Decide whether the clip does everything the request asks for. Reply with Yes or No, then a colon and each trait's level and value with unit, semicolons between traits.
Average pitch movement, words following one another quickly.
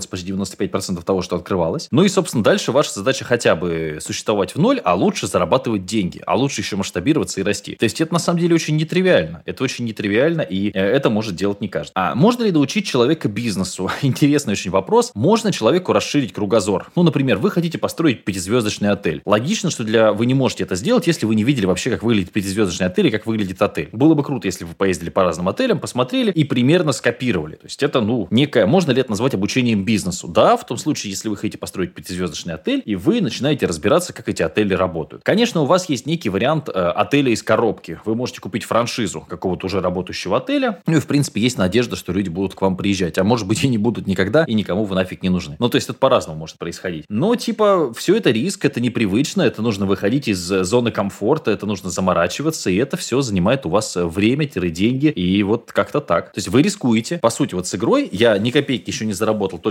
No: wide, 6.9 semitones; fast, 220 wpm